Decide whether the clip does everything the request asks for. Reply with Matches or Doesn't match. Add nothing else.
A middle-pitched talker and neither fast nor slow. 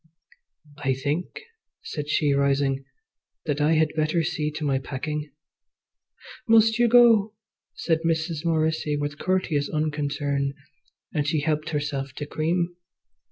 Doesn't match